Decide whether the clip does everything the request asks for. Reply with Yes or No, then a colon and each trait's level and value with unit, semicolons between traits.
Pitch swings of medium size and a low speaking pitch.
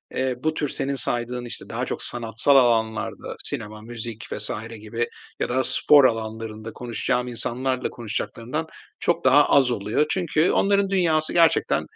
Yes: average, 4.4 semitones; low, 125 Hz